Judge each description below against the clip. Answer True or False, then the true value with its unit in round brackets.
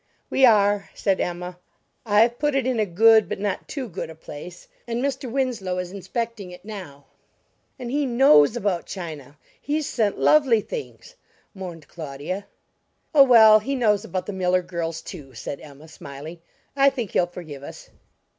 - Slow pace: False (165 wpm)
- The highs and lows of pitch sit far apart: True (5.7 semitones)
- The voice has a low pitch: False (200 Hz)